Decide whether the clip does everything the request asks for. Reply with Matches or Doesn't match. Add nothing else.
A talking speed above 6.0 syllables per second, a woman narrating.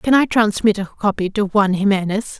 Doesn't match